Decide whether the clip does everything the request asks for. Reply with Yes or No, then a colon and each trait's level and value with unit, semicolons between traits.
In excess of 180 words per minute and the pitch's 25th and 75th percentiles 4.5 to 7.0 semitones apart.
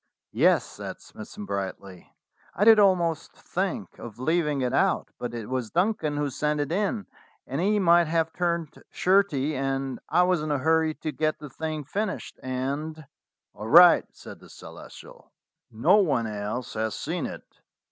No: average, 170 wpm; average, 5.0 semitones